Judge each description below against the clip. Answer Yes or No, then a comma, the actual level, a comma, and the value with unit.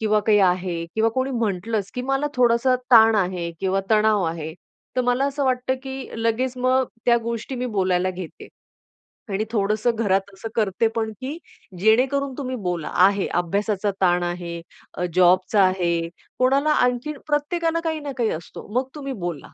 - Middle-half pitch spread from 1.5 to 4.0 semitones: No, wide, 5.5 semitones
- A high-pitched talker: Yes, high, 220 Hz